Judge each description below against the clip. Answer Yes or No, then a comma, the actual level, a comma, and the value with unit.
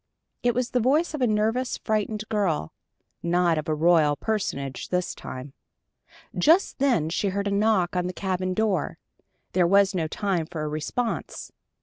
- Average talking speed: Yes, average, 165 wpm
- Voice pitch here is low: No, high, 190 Hz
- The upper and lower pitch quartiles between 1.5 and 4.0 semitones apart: No, average, 4.6 semitones